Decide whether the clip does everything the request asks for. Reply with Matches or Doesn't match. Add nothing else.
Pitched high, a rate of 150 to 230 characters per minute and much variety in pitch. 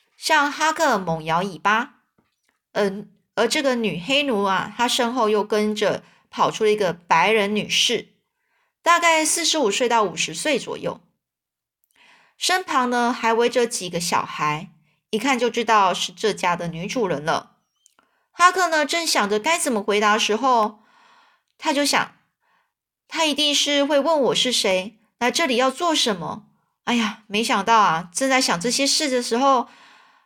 Matches